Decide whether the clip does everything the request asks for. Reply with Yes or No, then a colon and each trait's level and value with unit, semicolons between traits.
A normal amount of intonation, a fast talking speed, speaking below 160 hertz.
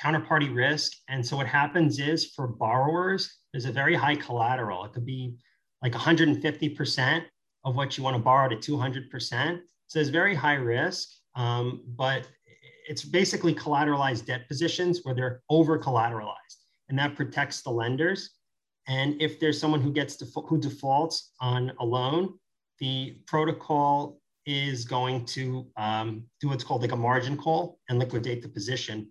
No: average, 3.6 semitones; average, 160 wpm; medium, 140 Hz